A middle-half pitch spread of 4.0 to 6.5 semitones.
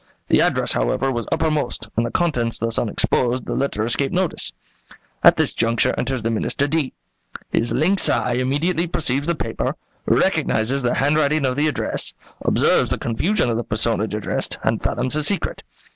Yes: average, 4.7 semitones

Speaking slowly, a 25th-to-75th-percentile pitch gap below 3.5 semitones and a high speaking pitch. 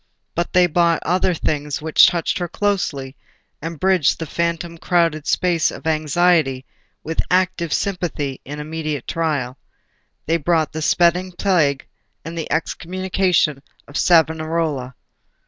No: slow, 130 wpm; average, 2.7 semitones; medium, 165 Hz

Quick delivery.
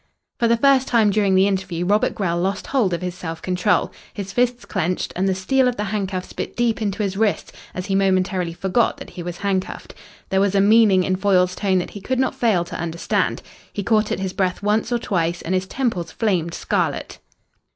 Yes: fast, 215 wpm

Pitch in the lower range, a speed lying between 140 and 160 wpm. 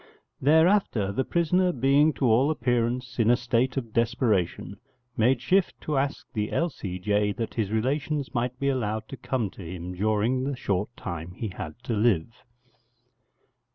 Yes: low, 120 Hz; average, 155 wpm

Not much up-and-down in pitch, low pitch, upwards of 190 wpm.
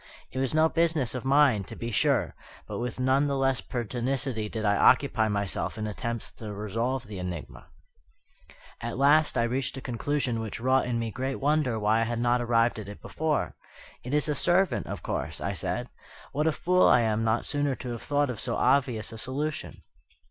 No: average, 3.8 semitones; low, 125 Hz; average, 200 wpm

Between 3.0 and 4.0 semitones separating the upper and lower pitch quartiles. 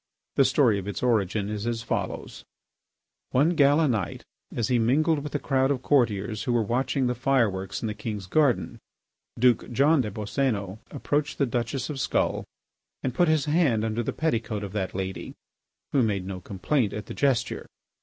No: average, 4.7 semitones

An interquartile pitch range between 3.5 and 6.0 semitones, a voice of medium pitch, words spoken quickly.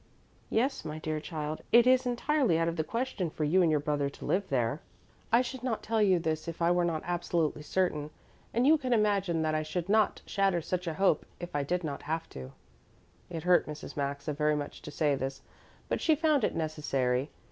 Yes: average, 5.1 semitones; medium, 165 Hz; fast, 215 wpm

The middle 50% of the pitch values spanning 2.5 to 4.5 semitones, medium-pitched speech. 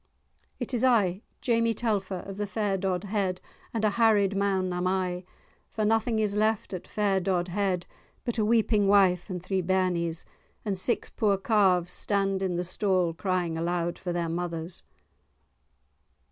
No: average, 2.8 semitones; high, 195 Hz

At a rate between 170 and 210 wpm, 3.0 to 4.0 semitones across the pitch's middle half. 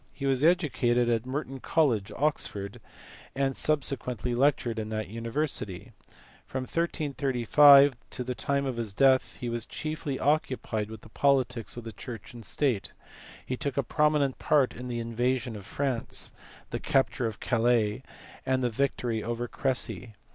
No: average, 155 wpm; average, 3.3 semitones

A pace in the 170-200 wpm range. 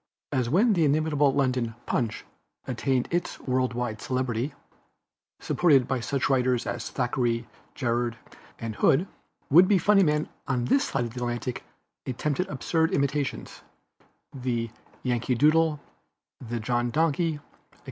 No: slow, 135 wpm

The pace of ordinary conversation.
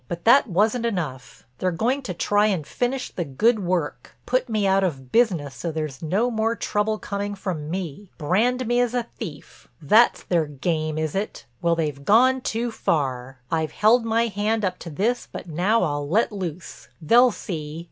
Yes: average, 170 wpm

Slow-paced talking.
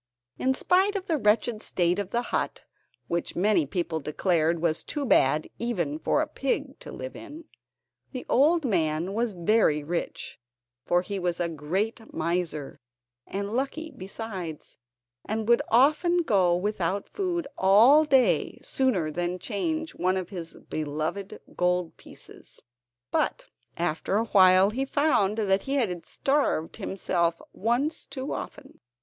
No: average, 145 wpm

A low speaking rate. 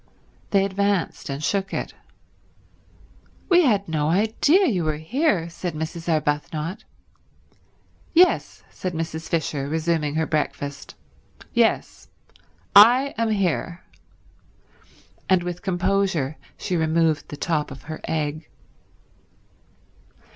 Yes: slow, 105 wpm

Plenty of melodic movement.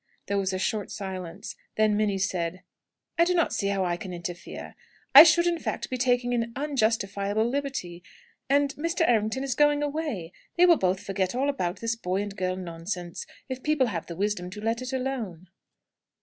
Yes: wide, 6.2 semitones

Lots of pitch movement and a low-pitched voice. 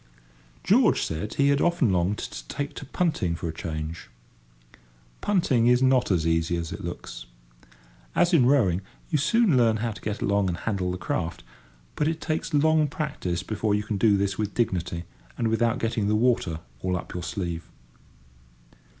Yes: wide, 7.4 semitones; low, 105 Hz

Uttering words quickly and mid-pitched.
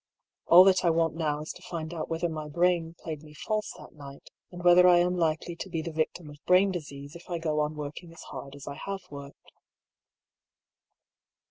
Yes: fast, 210 wpm; medium, 165 Hz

